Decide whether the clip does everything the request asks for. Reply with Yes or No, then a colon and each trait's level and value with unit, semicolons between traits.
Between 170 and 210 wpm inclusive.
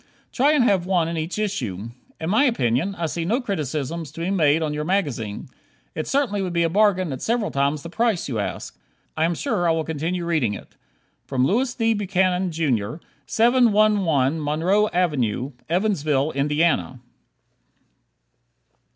No: average, 160 wpm